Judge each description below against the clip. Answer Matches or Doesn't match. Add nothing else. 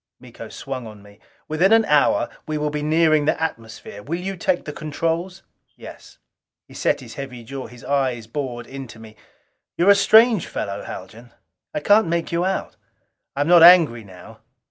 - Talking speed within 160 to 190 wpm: Matches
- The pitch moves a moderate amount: Doesn't match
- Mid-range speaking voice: Matches